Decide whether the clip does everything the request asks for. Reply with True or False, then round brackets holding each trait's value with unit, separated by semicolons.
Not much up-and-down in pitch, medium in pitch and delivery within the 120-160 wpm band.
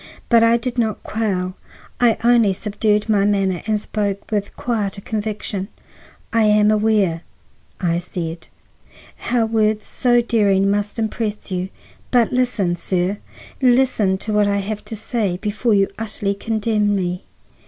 False (2.3 semitones; 210 Hz; 145 wpm)